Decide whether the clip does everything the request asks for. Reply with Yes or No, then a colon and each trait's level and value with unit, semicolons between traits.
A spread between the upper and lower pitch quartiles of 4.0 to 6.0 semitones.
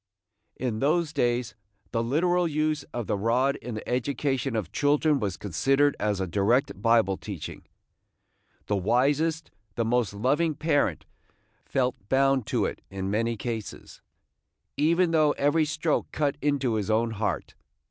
Yes: average, 5.2 semitones